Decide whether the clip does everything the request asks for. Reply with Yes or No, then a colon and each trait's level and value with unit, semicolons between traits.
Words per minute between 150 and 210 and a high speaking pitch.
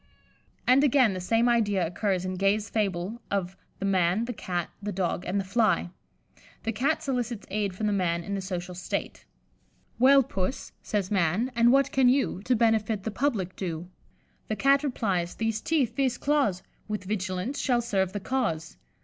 Yes: average, 175 wpm; high, 210 Hz